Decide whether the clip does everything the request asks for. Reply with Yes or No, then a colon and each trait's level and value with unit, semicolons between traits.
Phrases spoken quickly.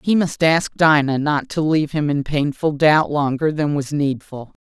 No: average, 195 wpm